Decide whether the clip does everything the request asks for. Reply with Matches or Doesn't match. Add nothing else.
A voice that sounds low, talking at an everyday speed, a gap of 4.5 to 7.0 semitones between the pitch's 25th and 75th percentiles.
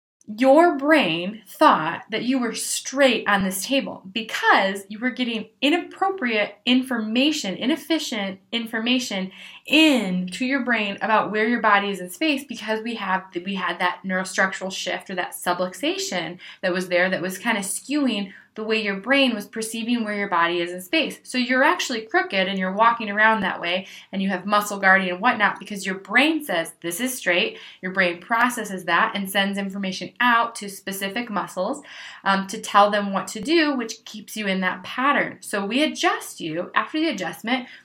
Doesn't match